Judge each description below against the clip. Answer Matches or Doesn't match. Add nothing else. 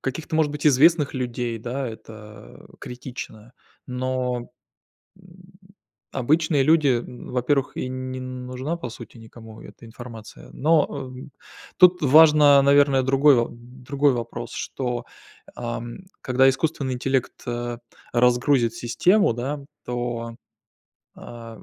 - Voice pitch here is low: Matches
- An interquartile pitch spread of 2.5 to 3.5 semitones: Matches